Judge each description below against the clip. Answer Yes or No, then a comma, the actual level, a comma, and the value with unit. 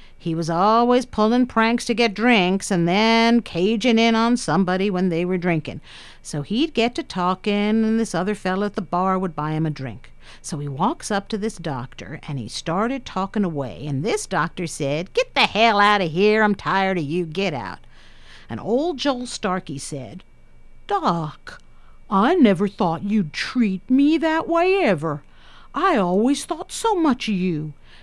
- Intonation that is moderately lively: No, wide, 5.9 semitones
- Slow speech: No, average, 180 wpm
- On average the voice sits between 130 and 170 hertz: No, high, 195 Hz